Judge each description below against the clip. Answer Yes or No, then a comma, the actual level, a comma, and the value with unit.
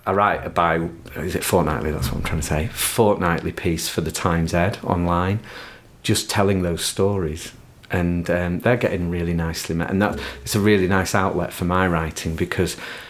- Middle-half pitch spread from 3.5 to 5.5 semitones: No, average, 2.9 semitones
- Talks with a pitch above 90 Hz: No, very low, 85 Hz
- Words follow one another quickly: No, average, 190 wpm